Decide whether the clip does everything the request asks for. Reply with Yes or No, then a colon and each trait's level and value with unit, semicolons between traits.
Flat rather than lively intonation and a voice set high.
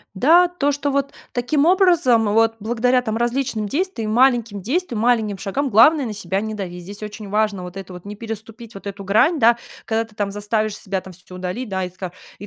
No: average, 4.0 semitones; high, 220 Hz